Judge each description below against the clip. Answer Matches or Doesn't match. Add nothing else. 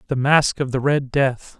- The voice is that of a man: Matches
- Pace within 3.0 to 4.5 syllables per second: Matches